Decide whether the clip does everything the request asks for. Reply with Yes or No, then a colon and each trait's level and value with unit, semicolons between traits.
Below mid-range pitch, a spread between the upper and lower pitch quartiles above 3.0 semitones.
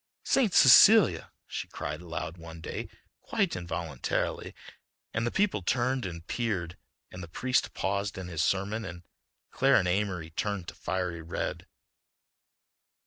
Yes: very low, 95 Hz; average, 5.3 semitones